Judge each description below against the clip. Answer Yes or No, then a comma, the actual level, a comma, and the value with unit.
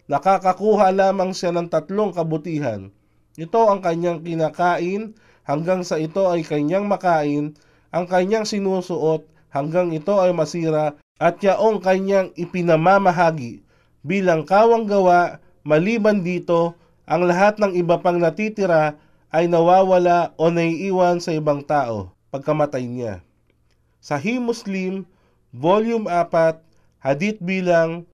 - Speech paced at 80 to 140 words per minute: Yes, average, 115 wpm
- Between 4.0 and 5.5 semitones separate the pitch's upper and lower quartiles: No, average, 3.4 semitones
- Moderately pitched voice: Yes, medium, 170 Hz